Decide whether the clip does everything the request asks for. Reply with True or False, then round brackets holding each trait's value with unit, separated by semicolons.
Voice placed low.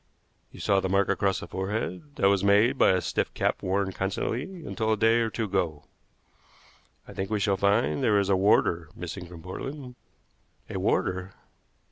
True (100 Hz)